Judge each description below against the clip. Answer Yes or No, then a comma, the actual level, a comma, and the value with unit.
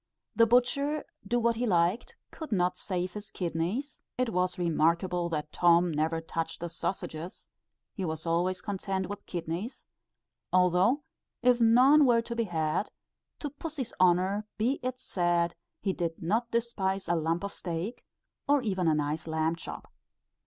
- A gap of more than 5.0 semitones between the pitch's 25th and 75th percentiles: Yes, wide, 5.6 semitones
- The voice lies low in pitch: No, medium, 185 Hz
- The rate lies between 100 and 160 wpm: Yes, average, 155 wpm